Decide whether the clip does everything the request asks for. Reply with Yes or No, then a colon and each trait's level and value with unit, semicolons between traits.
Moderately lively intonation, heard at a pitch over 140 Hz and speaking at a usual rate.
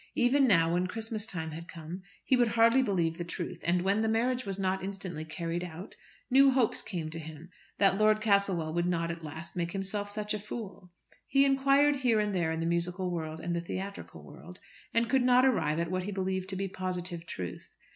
No: average, 4.4 semitones; high, 190 Hz; fast, 215 wpm